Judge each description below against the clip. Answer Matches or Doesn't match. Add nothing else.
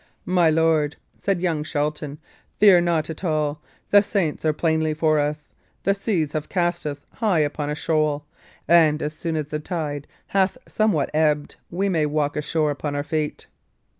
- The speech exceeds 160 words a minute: Matches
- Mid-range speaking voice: Matches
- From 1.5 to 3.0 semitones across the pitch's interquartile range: Matches